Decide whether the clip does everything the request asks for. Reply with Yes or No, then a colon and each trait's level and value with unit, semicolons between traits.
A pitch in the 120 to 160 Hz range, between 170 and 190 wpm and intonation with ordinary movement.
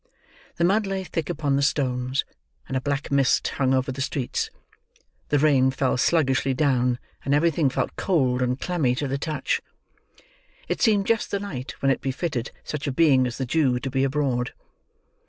Yes: medium, 140 Hz; average, 180 wpm; average, 3.2 semitones